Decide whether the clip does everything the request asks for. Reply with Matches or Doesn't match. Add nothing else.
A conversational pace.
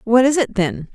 Doesn't match